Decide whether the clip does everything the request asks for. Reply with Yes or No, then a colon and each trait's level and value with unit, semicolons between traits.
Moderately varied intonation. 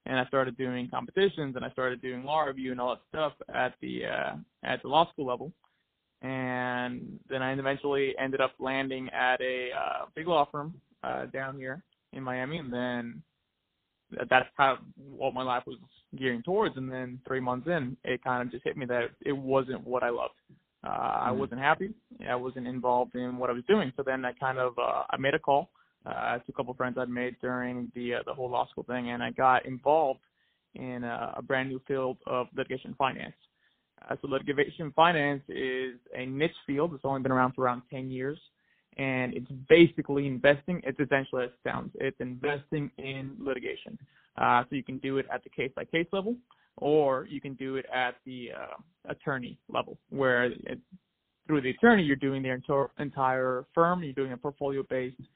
No: narrow, 2.0 semitones